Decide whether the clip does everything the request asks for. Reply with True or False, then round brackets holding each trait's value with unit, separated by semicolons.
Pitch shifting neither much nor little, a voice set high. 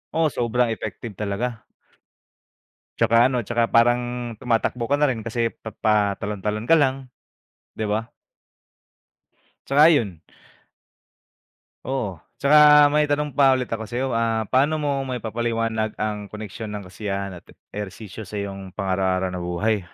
False (3.8 semitones; 115 Hz)